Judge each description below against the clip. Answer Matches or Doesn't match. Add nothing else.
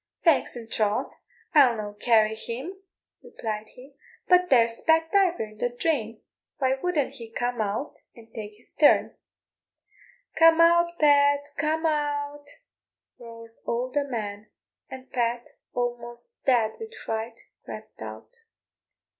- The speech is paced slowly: Matches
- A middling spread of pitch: Matches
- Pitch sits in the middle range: Doesn't match